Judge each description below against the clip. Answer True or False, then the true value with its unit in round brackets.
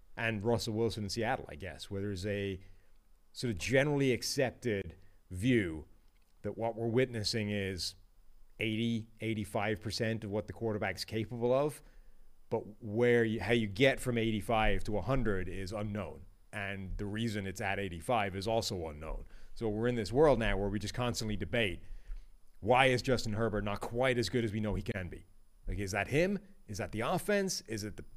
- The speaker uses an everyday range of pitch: True (3.1 semitones)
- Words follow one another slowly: False (185 wpm)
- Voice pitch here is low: True (110 Hz)